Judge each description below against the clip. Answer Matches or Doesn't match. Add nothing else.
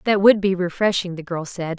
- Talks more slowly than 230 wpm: Doesn't match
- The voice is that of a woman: Matches